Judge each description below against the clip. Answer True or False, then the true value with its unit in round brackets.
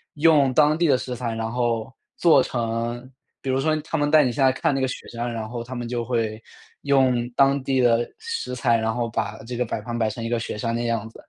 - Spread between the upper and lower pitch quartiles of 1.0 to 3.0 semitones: True (2.6 semitones)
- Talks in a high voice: False (120 Hz)